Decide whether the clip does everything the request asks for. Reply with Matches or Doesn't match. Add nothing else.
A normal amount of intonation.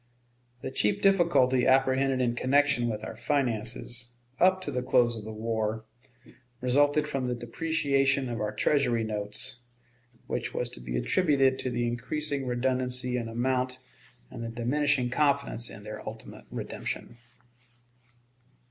Matches